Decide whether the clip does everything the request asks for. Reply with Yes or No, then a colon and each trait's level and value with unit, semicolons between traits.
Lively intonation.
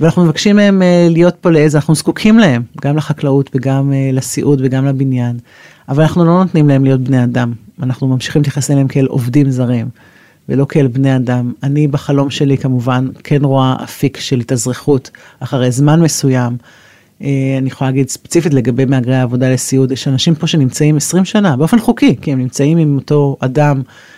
No: average, 2.8 semitones